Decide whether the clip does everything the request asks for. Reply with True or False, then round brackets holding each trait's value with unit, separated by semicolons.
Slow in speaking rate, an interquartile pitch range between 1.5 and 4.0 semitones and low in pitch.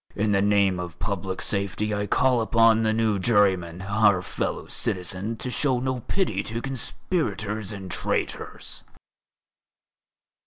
True (130 wpm; 2.9 semitones; 105 Hz)